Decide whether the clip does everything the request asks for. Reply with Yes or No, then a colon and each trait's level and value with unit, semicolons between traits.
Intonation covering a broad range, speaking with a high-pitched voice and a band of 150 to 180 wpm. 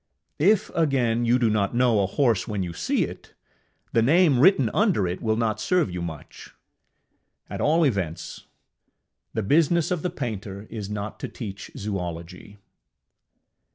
No: wide, 6.7 semitones; low, 115 Hz; average, 155 wpm